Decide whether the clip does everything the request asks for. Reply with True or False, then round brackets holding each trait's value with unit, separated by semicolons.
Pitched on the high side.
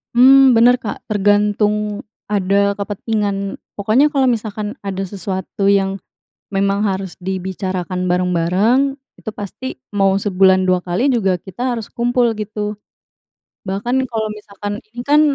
True (205 Hz)